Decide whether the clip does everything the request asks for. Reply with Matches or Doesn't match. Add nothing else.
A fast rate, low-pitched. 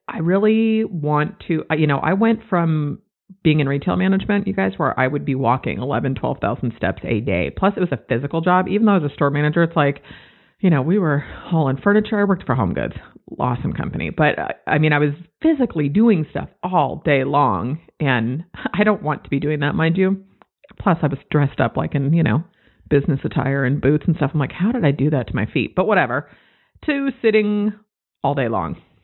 Doesn't match